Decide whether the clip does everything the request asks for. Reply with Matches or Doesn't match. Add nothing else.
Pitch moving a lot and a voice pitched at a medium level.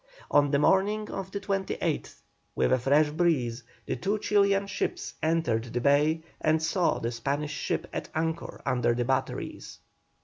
Matches